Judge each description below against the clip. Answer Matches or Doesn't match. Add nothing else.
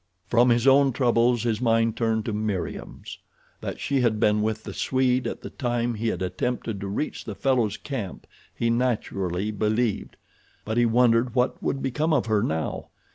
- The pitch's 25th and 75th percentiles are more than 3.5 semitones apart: Doesn't match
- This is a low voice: Matches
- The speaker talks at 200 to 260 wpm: Doesn't match